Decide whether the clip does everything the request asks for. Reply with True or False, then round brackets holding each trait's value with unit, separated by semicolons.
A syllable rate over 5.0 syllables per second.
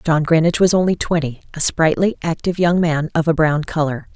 True (5.7 syllables/s)